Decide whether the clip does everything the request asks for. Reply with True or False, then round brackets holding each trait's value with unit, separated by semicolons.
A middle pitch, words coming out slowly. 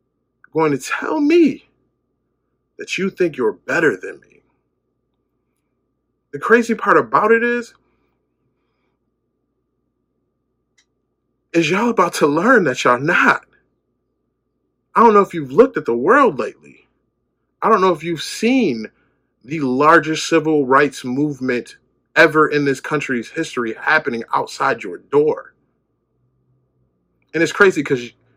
True (160 Hz; 125 wpm)